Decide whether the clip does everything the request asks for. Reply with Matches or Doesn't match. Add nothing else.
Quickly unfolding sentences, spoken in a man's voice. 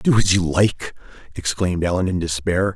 Doesn't match